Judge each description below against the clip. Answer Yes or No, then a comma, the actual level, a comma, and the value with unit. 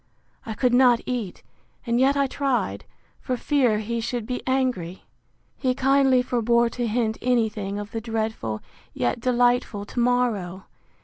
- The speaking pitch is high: Yes, high, 240 Hz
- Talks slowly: No, average, 150 wpm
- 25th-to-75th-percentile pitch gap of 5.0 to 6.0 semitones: No, average, 2.8 semitones